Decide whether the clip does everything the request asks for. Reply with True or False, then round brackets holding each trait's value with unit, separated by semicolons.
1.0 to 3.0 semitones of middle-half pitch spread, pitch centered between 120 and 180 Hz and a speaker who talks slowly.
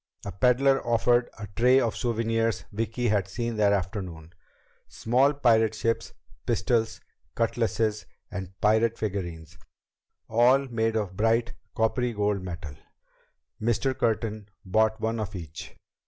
False (2.7 semitones; 110 Hz; 125 wpm)